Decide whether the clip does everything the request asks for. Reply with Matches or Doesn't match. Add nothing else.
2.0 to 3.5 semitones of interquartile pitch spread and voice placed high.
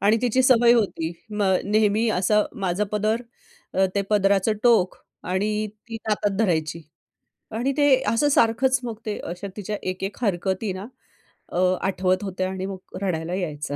Matches